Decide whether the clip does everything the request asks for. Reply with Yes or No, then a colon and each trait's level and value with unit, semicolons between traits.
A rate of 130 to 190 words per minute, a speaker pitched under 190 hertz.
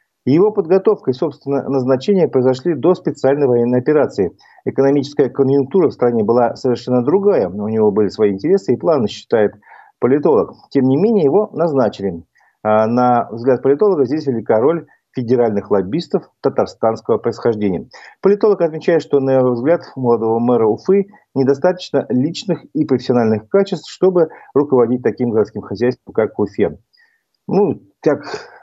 Yes: average, 140 wpm; low, 135 Hz